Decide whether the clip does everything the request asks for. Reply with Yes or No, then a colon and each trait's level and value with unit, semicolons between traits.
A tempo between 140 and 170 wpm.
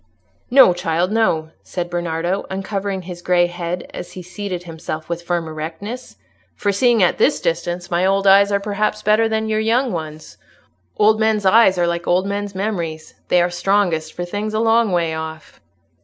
No: average, 180 wpm